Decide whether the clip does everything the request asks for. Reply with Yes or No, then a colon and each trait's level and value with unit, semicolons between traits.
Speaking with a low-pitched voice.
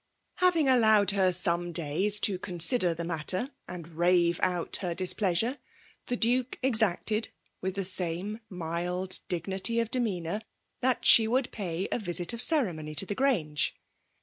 No: medium, 185 Hz